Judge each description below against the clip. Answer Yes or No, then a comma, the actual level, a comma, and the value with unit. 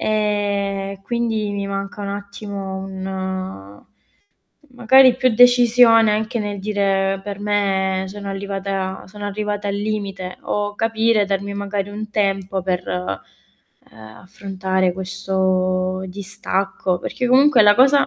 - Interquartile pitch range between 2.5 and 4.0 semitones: No, narrow, 1.8 semitones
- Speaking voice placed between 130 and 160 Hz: No, high, 200 Hz